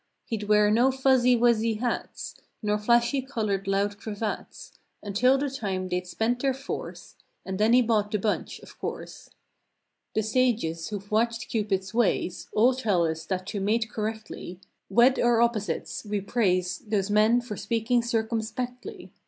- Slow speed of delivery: No, average, 155 wpm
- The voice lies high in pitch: Yes, high, 220 Hz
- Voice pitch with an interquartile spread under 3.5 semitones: Yes, average, 2.9 semitones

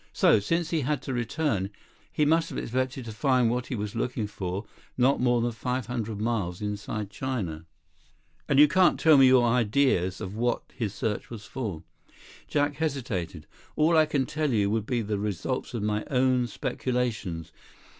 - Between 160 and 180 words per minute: Yes, average, 175 wpm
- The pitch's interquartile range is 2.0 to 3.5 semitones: No, average, 4.2 semitones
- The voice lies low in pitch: Yes, low, 120 Hz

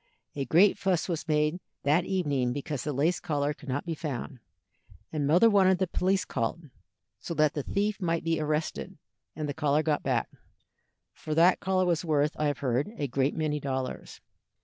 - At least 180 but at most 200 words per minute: Yes, average, 185 wpm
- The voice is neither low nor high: Yes, medium, 155 Hz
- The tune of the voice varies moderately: Yes, average, 3.4 semitones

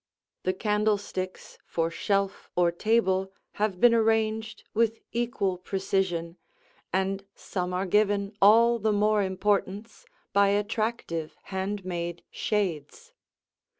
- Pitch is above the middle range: Yes, high, 200 Hz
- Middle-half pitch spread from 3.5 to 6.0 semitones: No, narrow, 2.6 semitones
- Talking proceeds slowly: Yes, slow, 110 wpm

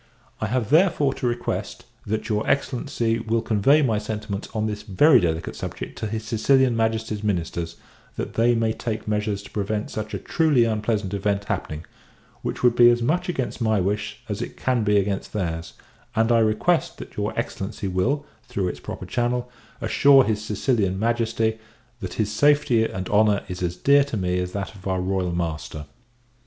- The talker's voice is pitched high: No, low, 110 Hz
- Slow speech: No, average, 180 wpm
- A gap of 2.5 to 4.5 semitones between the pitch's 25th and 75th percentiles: Yes, average, 3.3 semitones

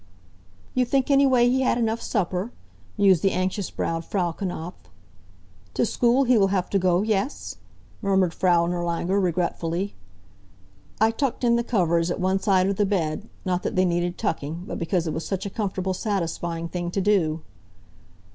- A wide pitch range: No, average, 3.5 semitones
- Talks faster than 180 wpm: No, average, 170 wpm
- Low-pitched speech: No, high, 190 Hz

